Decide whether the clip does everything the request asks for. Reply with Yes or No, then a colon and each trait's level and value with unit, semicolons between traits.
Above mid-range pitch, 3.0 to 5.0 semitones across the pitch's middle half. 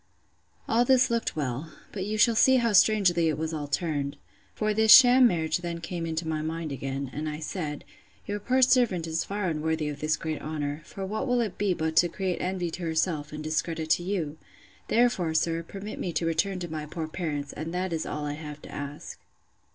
No: medium, 165 Hz; average, 4.3 semitones